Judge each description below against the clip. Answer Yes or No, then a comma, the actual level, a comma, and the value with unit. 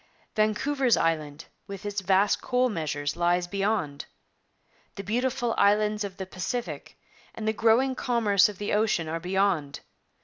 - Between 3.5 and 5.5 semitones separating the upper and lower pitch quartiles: Yes, average, 4.1 semitones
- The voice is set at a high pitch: Yes, high, 200 Hz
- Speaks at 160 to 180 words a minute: No, average, 140 wpm